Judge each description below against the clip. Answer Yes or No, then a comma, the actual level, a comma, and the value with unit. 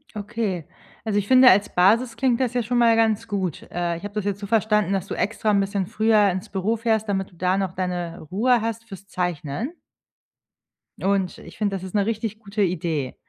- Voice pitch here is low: No, high, 205 Hz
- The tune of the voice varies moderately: Yes, average, 3.2 semitones